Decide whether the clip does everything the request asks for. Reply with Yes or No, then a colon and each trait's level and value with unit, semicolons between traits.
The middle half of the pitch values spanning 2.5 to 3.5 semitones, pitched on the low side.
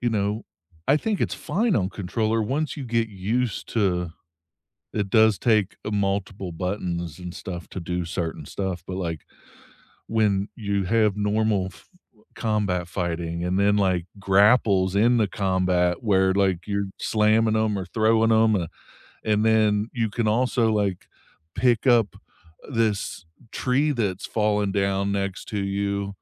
Yes: average, 2.8 semitones; low, 100 Hz